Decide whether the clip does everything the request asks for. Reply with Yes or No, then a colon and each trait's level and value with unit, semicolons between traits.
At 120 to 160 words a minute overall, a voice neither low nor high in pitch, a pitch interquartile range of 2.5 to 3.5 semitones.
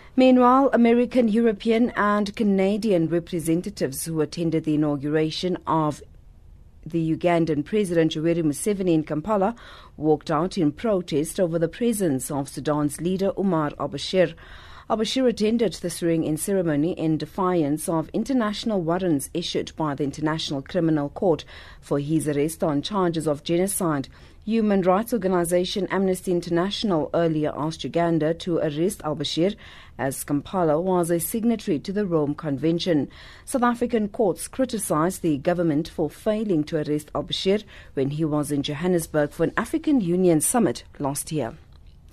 No: average, 140 wpm; medium, 170 Hz; average, 4.3 semitones